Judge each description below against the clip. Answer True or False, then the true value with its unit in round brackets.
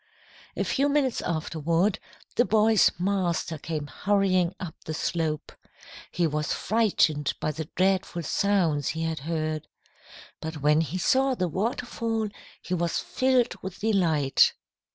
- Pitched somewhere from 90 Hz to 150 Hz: False (175 Hz)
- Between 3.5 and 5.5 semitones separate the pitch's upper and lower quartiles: True (4.7 semitones)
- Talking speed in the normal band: False (130 wpm)